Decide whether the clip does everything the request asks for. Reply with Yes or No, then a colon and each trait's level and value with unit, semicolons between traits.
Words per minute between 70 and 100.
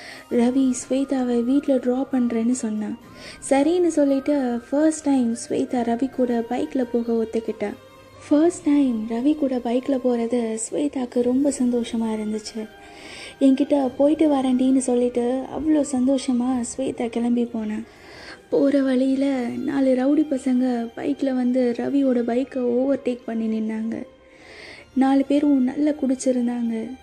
No: average, 115 wpm